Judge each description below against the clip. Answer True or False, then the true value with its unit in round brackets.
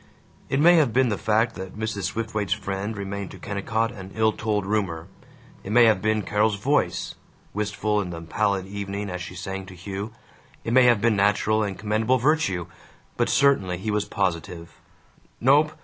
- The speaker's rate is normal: True (180 wpm)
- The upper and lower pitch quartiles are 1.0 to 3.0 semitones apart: True (2.6 semitones)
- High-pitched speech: False (105 Hz)